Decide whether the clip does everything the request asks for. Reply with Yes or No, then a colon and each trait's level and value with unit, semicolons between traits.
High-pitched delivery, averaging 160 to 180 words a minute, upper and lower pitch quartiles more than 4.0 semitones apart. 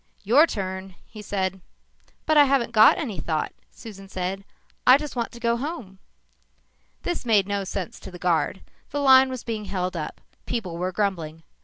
Yes: high, 200 Hz; average, 175 wpm; average, 4.6 semitones